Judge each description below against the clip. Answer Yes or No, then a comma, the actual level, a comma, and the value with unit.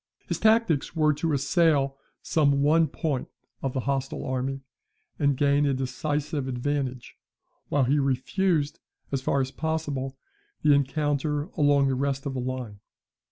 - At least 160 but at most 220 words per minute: No, average, 145 wpm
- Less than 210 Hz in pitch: Yes, medium, 140 Hz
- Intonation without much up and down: Yes, narrow, 2.1 semitones